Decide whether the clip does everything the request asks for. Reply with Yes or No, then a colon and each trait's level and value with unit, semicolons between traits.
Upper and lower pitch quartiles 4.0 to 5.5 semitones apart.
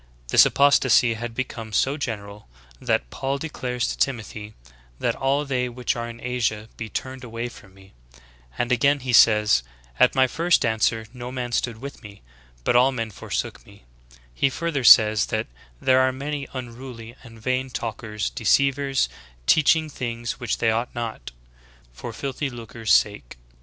No: average, 3.1 semitones